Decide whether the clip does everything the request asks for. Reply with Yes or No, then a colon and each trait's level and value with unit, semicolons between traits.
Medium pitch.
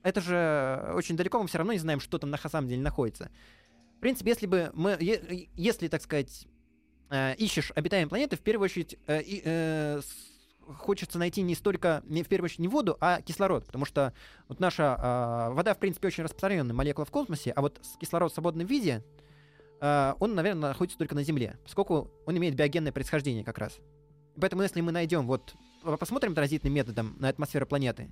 Yes: medium, 155 Hz